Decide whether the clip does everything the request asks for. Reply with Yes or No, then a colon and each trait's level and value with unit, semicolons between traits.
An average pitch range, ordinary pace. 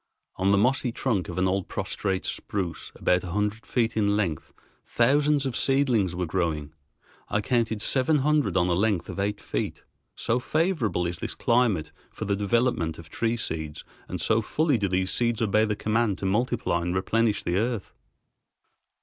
Yes: average, 4.3 semitones; average, 175 wpm